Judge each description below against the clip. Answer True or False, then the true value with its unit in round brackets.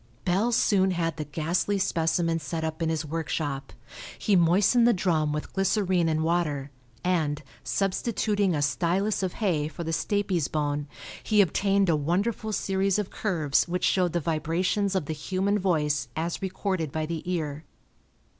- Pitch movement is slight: False (3.7 semitones)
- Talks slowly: False (160 wpm)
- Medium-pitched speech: True (170 Hz)